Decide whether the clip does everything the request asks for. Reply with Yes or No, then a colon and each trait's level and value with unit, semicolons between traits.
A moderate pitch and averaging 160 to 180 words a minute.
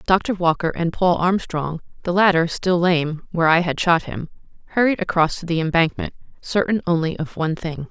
Yes: medium, 170 Hz; average, 165 wpm